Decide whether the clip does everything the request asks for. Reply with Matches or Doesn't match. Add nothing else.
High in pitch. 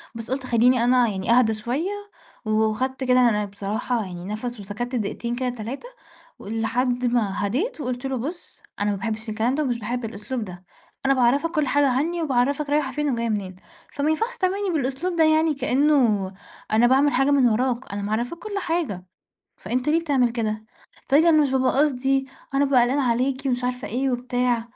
Matches